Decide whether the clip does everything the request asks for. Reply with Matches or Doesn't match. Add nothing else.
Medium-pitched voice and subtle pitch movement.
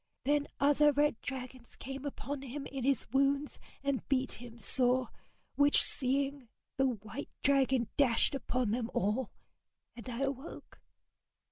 Doesn't match